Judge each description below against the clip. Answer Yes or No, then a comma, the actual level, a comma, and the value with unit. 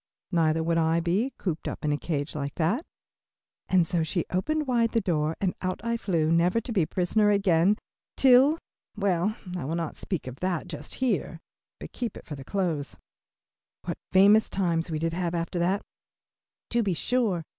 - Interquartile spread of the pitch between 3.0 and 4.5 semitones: Yes, average, 4.2 semitones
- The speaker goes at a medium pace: Yes, average, 190 wpm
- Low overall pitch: No, medium, 175 Hz